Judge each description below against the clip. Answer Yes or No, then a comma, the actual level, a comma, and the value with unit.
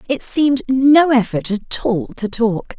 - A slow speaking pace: No, average, 170 wpm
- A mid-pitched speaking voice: No, high, 240 Hz